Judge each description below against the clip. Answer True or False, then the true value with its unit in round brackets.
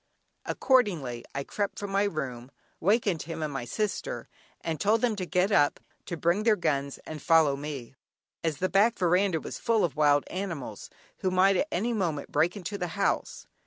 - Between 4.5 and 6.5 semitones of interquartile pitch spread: True (5.2 semitones)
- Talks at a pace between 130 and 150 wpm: False (185 wpm)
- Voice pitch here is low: False (175 Hz)